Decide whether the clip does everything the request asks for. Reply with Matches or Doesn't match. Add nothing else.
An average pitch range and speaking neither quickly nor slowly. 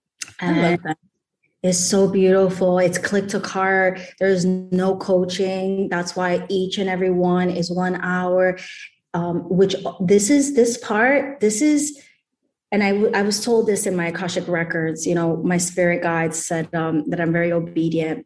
Doesn't match